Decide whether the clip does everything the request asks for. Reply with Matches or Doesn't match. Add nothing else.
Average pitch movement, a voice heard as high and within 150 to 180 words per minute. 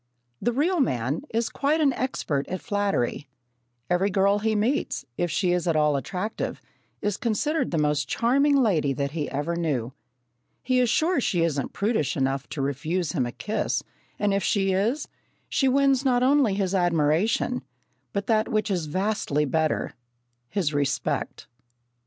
Doesn't match